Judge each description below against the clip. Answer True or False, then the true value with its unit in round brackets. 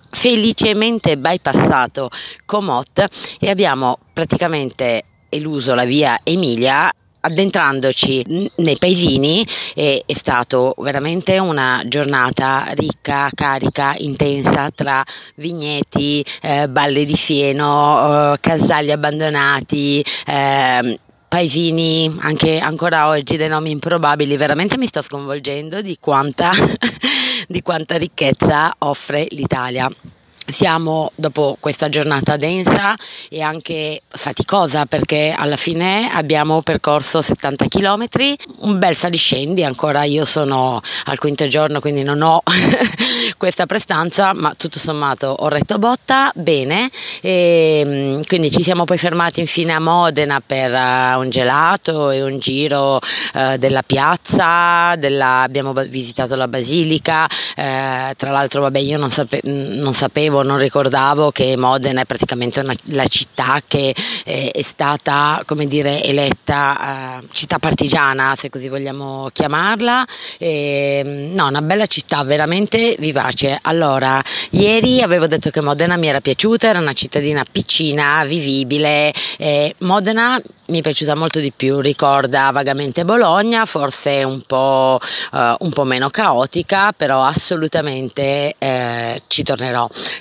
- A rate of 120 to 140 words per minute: True (125 wpm)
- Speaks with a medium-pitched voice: True (150 Hz)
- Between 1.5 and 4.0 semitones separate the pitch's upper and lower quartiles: True (3.5 semitones)